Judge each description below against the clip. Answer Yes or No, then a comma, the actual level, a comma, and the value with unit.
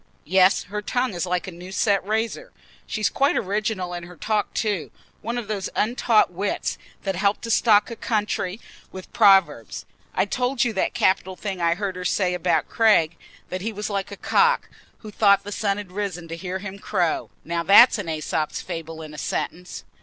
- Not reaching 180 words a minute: No, average, 190 wpm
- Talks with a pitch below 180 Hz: No, high, 195 Hz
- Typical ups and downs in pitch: Yes, average, 3.1 semitones